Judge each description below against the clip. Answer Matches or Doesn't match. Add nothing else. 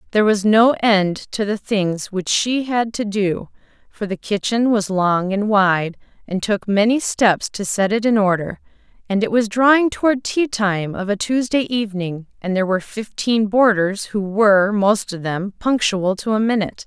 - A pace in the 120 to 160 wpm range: Doesn't match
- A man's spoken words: Doesn't match